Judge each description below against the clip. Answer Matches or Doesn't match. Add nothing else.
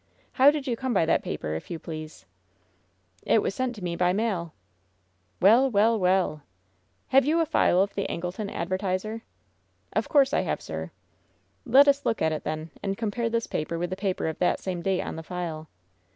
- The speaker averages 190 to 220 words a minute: Matches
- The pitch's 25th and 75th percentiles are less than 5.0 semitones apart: Doesn't match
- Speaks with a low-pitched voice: Doesn't match